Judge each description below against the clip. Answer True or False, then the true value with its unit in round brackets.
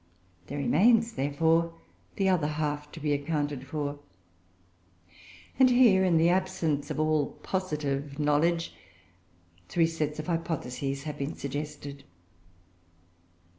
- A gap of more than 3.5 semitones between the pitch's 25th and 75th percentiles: False (2.7 semitones)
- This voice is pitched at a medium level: True (150 Hz)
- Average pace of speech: False (115 wpm)